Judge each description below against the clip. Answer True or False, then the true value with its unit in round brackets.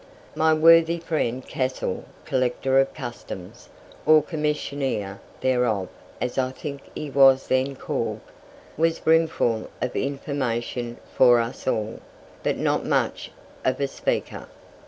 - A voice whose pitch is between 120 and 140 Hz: True (135 Hz)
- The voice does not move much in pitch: False (3.7 semitones)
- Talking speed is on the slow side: True (120 wpm)